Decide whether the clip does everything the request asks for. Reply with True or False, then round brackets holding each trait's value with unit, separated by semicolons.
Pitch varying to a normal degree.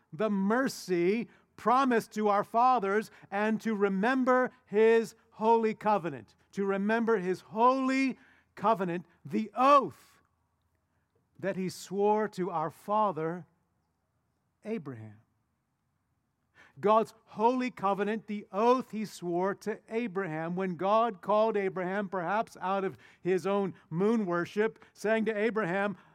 True (3.8 semitones)